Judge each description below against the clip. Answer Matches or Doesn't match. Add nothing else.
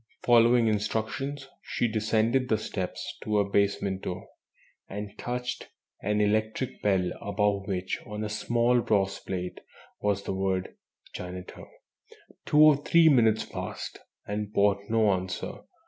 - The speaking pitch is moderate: Doesn't match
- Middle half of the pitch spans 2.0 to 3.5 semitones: Matches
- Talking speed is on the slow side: Matches